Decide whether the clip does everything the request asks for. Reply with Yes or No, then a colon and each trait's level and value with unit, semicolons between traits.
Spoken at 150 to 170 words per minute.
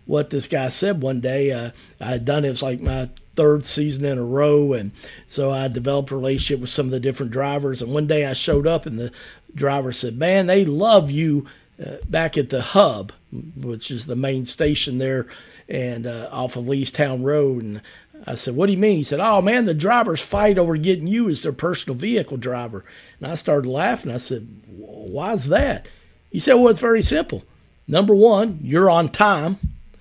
No: fast, 205 wpm